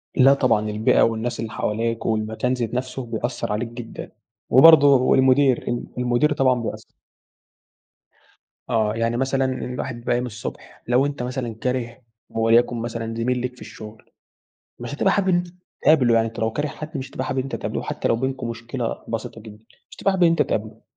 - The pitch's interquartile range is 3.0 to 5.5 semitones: No, narrow, 2.5 semitones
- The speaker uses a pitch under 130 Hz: Yes, low, 120 Hz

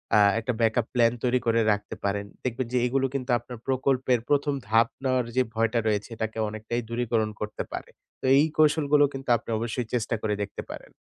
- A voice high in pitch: No, low, 120 Hz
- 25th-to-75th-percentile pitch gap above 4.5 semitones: No, average, 2.7 semitones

